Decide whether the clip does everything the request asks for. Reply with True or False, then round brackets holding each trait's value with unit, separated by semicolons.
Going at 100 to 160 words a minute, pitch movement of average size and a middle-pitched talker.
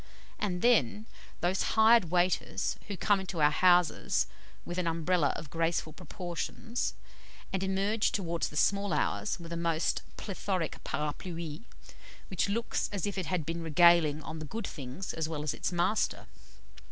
True (155 wpm; 3.3 semitones; 175 Hz)